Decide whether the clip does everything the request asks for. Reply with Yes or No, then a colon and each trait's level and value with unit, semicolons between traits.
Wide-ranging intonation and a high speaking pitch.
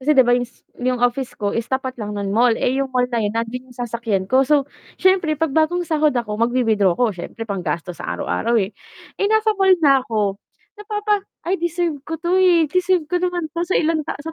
Yes: wide, 7.1 semitones; very high, 260 Hz